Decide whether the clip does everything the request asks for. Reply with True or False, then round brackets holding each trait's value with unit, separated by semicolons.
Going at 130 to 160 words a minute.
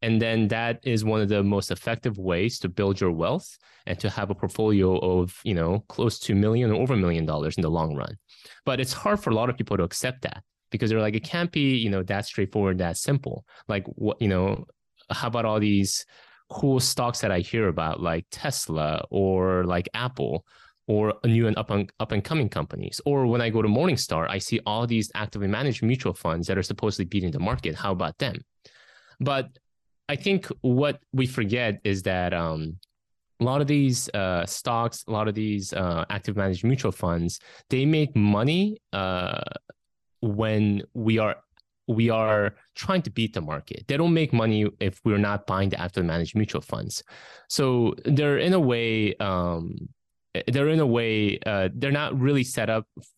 False (200 wpm)